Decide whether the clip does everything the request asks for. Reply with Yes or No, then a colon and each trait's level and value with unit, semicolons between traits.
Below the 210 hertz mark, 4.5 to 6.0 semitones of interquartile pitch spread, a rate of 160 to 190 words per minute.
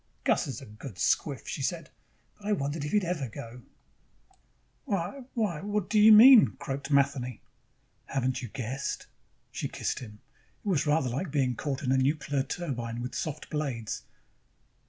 Yes: medium, 140 Hz; wide, 5.4 semitones; average, 165 wpm